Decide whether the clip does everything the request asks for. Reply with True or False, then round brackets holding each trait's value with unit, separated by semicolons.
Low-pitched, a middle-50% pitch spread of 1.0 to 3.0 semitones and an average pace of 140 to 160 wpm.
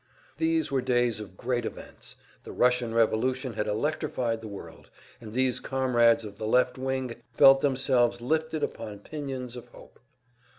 True (125 Hz; 2.5 semitones; 155 wpm)